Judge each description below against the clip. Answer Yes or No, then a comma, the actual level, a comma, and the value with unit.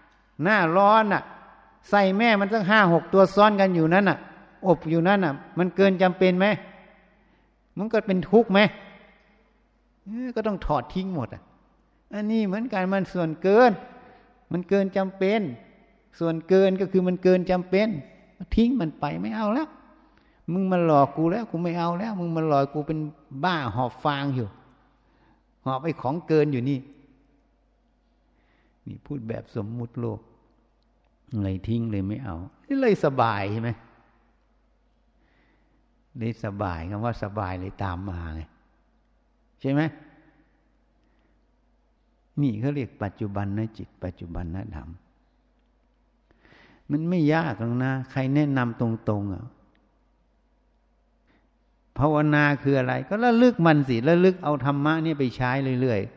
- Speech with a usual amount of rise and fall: No, wide, 8.2 semitones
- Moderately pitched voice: Yes, medium, 155 Hz